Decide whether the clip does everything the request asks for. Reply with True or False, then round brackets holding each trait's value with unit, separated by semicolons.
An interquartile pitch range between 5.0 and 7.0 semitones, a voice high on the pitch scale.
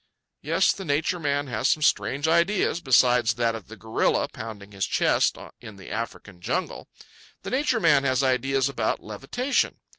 False (5.6 semitones; 130 Hz)